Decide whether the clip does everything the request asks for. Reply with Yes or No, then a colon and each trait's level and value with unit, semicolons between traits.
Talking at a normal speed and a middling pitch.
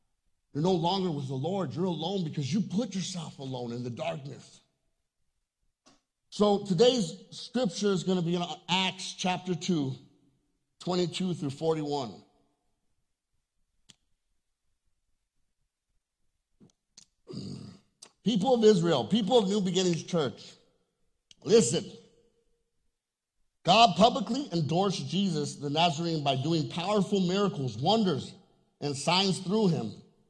No: slow, 105 wpm; medium, 180 Hz